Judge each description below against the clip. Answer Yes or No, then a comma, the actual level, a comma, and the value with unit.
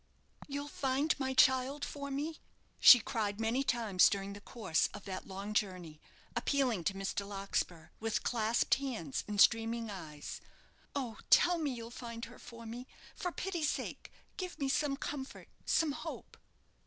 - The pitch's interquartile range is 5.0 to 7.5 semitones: Yes, wide, 5.4 semitones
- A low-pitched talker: No, high, 235 Hz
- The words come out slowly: No, average, 160 wpm